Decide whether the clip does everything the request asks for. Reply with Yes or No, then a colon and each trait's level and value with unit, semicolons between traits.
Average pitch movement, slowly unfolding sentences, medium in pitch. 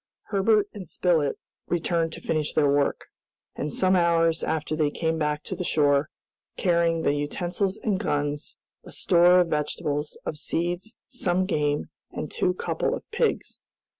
No: average, 3.3 semitones; average, 155 wpm; medium, 165 Hz